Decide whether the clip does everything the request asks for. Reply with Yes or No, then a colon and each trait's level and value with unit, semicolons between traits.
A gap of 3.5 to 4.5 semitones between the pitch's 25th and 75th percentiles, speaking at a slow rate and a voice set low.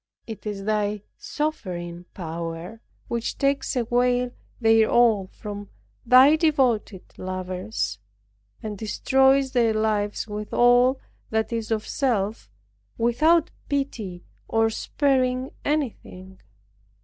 No: average, 3.9 semitones; slow, 100 wpm; high, 225 Hz